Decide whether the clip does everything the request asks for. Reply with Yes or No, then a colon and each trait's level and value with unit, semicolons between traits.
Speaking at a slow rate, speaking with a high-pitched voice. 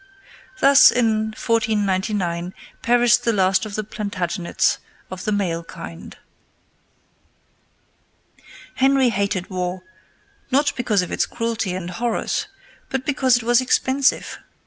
Yes: slow, 115 wpm; high, 215 Hz